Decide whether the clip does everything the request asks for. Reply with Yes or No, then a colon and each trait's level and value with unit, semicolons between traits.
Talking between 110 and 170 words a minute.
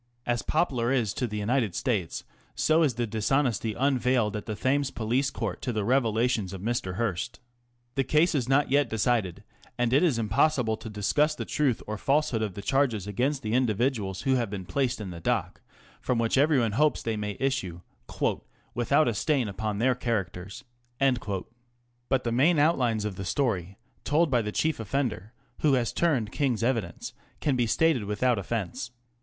No: average, 180 wpm